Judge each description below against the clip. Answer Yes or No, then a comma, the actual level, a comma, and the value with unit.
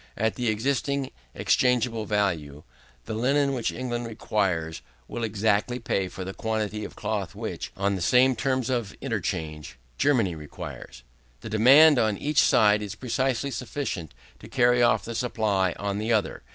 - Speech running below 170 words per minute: Yes, average, 155 wpm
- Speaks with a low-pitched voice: Yes, low, 110 Hz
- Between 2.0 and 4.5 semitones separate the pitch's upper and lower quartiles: Yes, average, 3.9 semitones